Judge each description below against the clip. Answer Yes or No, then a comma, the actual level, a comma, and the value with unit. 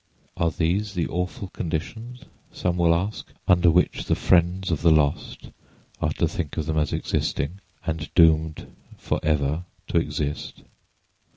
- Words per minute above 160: No, average, 145 wpm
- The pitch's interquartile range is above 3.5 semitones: No, narrow, 2.4 semitones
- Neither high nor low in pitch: No, very low, 85 Hz